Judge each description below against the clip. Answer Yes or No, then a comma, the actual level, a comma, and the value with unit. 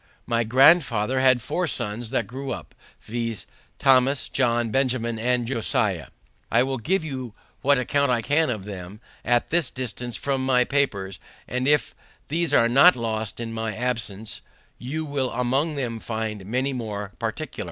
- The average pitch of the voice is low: Yes, low, 125 Hz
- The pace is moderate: Yes, average, 160 wpm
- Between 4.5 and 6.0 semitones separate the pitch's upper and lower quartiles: No, average, 3.2 semitones